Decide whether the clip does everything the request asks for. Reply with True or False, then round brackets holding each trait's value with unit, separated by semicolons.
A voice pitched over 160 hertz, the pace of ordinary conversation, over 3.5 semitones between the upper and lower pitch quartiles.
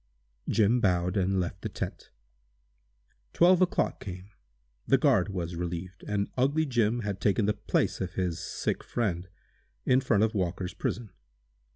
False (100 Hz; 150 wpm; 4.4 semitones)